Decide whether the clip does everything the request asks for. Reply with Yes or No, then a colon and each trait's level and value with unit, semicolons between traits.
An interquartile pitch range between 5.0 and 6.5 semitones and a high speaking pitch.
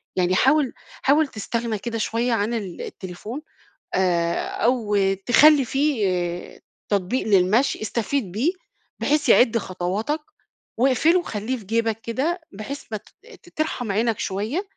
Yes: average, 5.3 semitones; high, 230 Hz